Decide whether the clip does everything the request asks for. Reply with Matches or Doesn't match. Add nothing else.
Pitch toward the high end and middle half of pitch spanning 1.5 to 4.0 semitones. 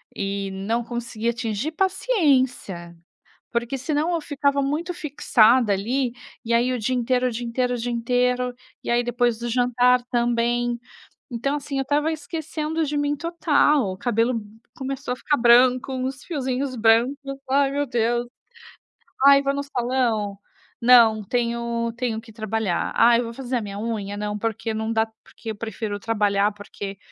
Matches